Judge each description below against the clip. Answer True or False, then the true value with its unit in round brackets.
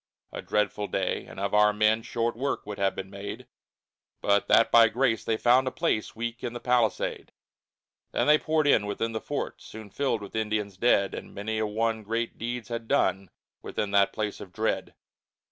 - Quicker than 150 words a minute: True (195 wpm)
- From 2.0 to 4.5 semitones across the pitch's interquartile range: True (2.4 semitones)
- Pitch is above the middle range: False (110 Hz)